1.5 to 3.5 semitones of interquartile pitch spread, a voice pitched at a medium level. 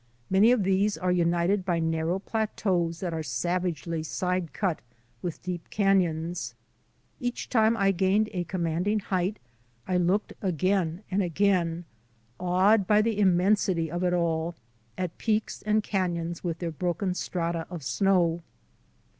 Yes: narrow, 2.6 semitones; medium, 180 Hz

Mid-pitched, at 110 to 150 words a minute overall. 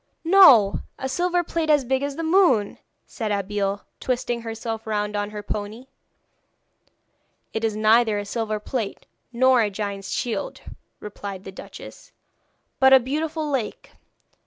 No: high, 225 Hz; average, 140 wpm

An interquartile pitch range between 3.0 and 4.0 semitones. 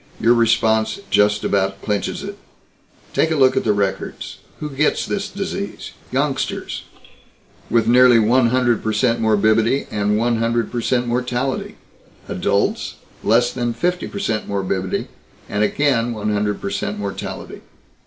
Yes: average, 3.3 semitones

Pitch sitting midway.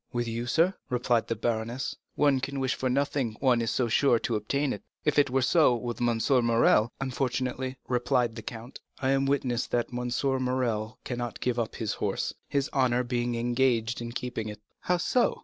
No: low, 125 Hz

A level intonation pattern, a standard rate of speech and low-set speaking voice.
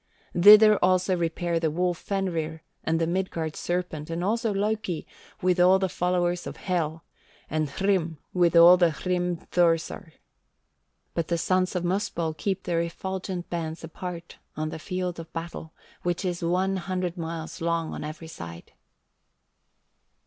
No: narrow, 2.0 semitones; average, 145 wpm; medium, 175 Hz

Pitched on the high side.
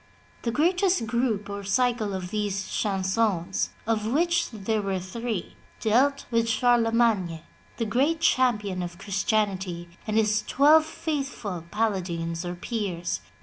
Yes: high, 215 Hz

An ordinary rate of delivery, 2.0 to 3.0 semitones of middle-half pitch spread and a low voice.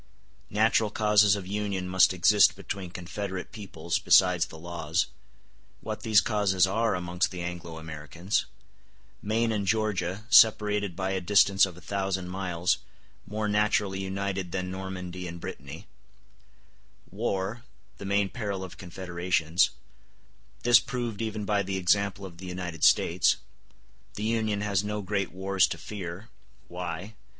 No: slow, 125 wpm; narrow, 2.6 semitones; very low, 95 Hz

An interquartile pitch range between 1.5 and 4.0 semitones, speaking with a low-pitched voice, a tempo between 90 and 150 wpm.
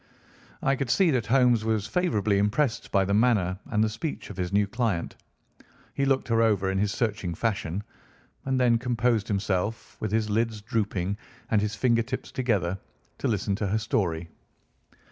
No: average, 3.2 semitones; low, 110 Hz; average, 170 wpm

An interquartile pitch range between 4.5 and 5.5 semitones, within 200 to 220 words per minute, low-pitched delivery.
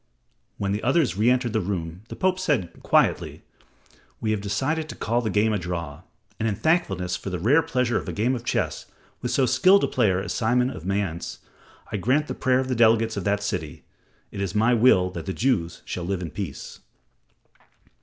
Yes: average, 5.0 semitones; fast, 205 wpm; low, 110 Hz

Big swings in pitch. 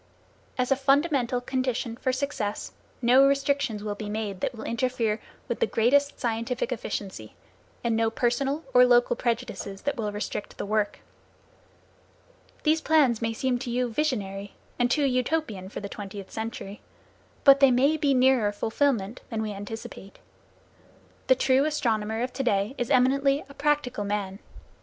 No: average, 4.3 semitones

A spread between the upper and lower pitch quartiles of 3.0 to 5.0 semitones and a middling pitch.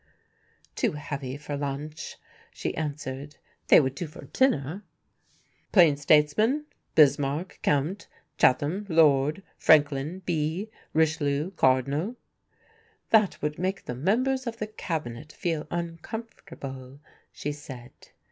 Yes: average, 4.5 semitones; medium, 150 Hz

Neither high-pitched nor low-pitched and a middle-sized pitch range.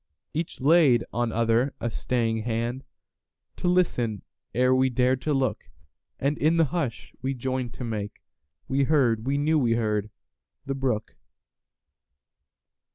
No: low, 125 Hz; average, 3.3 semitones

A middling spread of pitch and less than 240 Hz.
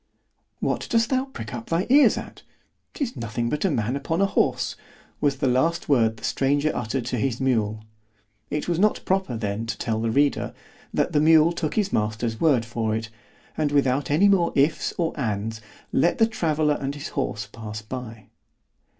No: wide, 6.3 semitones; low, 135 Hz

